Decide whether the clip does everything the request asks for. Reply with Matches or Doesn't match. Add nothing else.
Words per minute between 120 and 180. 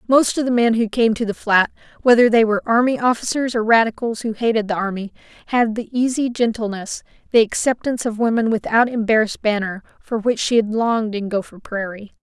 Doesn't match